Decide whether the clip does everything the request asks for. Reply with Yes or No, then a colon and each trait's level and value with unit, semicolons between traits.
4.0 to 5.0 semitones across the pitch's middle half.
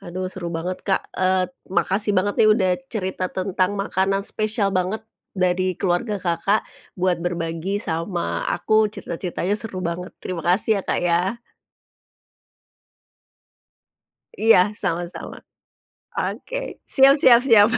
No: average, 2.8 semitones